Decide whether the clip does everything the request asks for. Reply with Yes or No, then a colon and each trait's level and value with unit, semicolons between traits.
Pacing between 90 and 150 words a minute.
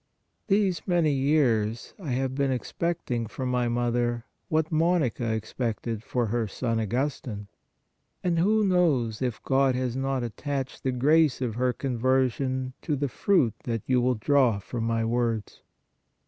Yes: average, 145 wpm